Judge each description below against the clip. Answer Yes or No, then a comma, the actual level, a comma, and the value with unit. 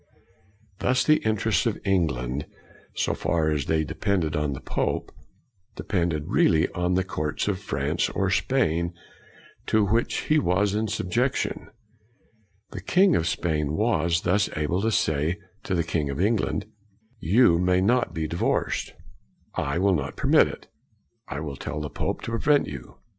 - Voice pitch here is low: Yes, very low, 90 Hz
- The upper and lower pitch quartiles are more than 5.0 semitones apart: Yes, wide, 5.6 semitones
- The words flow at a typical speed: Yes, average, 160 wpm